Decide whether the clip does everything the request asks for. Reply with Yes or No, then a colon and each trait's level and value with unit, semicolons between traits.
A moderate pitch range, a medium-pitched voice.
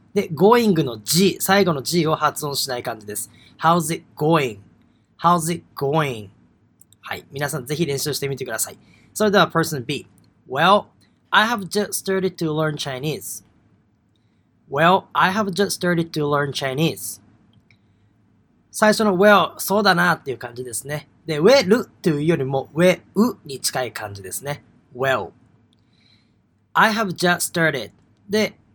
No: wide, 6.6 semitones; medium, 150 Hz